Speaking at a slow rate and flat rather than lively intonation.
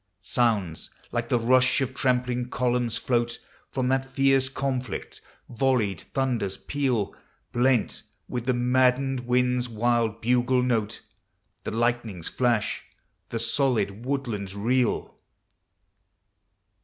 Yes: slow, 105 wpm; narrow, 2.1 semitones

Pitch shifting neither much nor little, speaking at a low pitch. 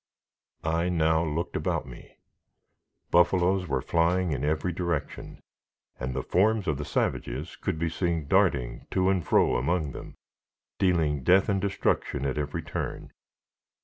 Yes: average, 3.9 semitones; very low, 85 Hz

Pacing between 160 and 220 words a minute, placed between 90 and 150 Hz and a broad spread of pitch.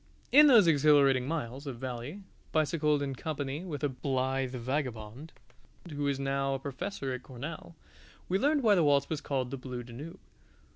No: average, 165 wpm; medium, 140 Hz; average, 3.1 semitones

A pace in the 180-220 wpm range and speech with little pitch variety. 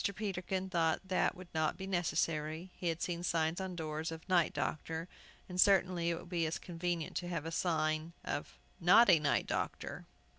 Yes: average, 185 wpm; narrow, 2.3 semitones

